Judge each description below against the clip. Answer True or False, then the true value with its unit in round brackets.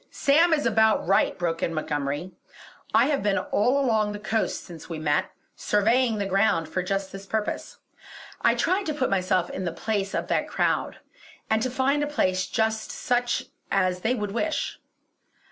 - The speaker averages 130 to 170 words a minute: False (180 wpm)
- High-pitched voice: True (210 Hz)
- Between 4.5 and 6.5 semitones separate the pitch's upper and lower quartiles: True (4.9 semitones)